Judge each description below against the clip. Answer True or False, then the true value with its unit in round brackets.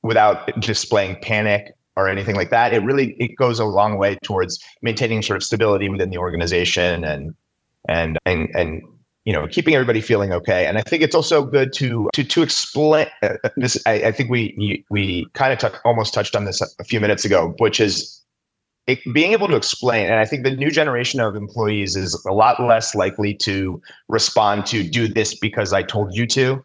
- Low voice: True (110 Hz)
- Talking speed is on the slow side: False (205 wpm)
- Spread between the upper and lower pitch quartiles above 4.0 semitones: True (4.4 semitones)